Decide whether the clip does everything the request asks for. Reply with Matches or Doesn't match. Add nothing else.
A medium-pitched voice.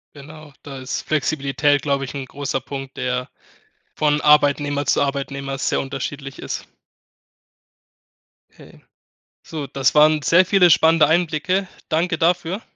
Matches